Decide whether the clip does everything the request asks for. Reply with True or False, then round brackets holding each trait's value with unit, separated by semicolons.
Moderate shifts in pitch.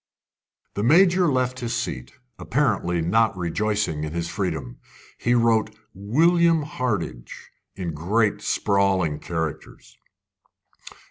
False (6.5 semitones)